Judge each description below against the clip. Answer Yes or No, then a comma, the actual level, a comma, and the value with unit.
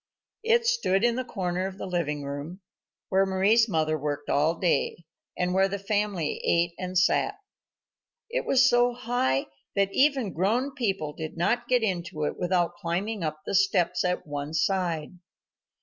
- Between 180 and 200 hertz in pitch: Yes, medium, 185 Hz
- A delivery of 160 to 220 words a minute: Yes, average, 165 wpm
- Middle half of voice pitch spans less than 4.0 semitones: No, average, 5.0 semitones